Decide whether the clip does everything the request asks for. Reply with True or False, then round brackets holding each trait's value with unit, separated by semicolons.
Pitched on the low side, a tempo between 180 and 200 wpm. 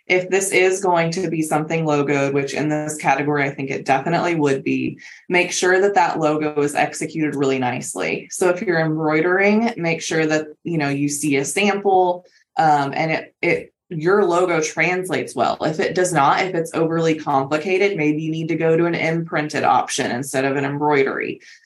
False (160 Hz; 190 wpm)